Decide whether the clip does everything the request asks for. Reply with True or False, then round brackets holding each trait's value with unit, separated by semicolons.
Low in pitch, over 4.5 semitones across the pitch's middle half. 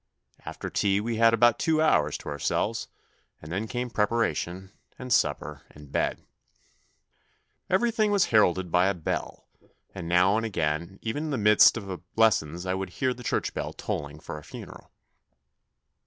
True (100 Hz; 5.3 semitones)